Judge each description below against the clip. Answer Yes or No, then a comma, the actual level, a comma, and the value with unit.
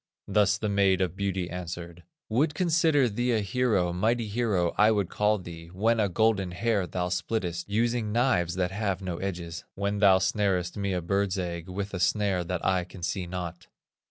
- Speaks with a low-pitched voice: Yes, very low, 95 Hz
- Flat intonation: No, average, 3.2 semitones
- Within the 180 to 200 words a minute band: Yes, average, 185 wpm